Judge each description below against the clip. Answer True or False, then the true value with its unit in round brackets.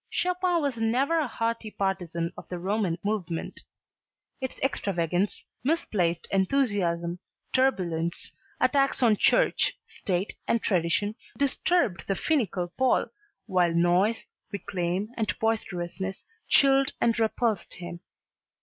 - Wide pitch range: True (6.2 semitones)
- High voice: True (205 Hz)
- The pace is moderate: False (110 wpm)